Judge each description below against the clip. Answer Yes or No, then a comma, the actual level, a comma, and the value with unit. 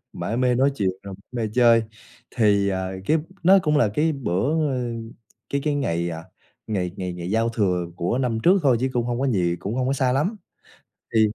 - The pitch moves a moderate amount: No, wide, 5.9 semitones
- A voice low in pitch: Yes, low, 120 Hz